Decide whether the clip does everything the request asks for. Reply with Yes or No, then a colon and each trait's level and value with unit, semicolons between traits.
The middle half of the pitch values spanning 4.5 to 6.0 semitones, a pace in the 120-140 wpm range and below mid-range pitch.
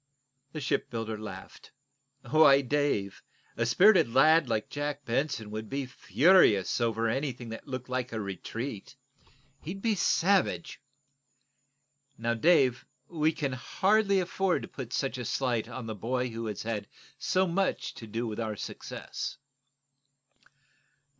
Yes: average, 5.3 semitones; slow, 135 wpm; low, 125 Hz